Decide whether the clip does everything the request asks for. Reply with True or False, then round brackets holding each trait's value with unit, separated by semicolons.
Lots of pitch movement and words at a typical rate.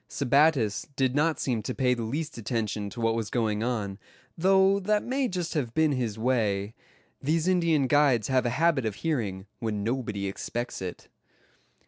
True (6.1 semitones; 170 wpm)